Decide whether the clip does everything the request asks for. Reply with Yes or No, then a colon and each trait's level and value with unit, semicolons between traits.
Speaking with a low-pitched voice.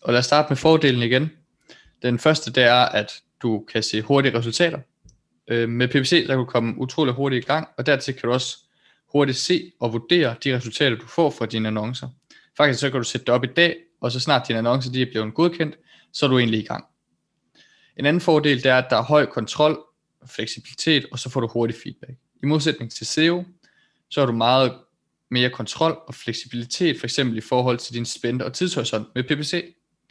Yes: low, 130 Hz